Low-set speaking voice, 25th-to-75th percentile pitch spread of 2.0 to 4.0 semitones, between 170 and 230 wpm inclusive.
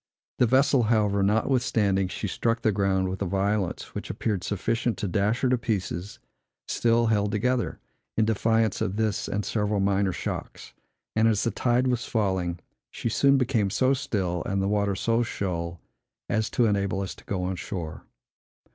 Yes: low, 105 Hz; average, 3.0 semitones; average, 175 wpm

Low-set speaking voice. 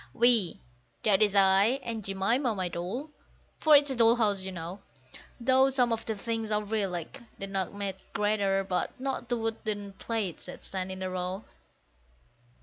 No: high, 205 Hz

